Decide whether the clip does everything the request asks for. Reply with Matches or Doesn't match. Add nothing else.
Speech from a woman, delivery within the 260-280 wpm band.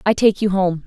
Matches